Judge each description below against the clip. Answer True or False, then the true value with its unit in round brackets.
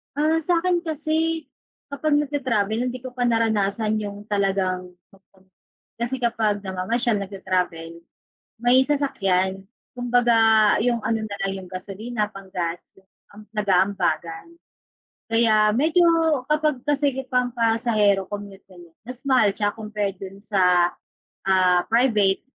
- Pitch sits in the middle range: False (215 Hz)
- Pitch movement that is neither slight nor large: True (4.2 semitones)